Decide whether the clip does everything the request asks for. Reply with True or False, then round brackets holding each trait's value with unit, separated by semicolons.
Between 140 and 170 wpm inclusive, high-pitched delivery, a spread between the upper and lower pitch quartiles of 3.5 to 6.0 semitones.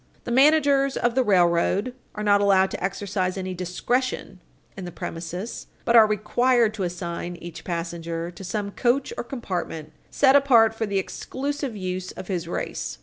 True (165 wpm; 200 Hz; 5.2 semitones)